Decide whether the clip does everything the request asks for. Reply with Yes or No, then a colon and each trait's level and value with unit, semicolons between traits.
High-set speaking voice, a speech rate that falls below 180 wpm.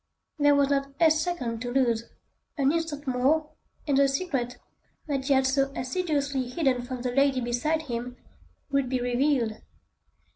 Yes: very high, 270 Hz; average, 155 wpm